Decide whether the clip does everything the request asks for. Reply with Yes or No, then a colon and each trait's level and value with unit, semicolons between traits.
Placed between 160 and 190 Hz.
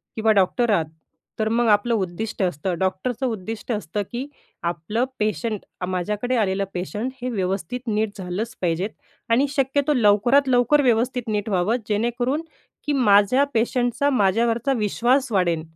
No: high, 220 Hz